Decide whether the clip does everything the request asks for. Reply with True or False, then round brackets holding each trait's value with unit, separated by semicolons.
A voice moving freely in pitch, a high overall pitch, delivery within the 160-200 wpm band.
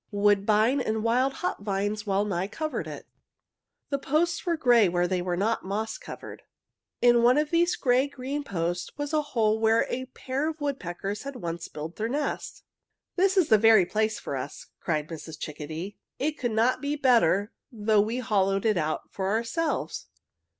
True (5.7 semitones; 220 Hz; 175 wpm)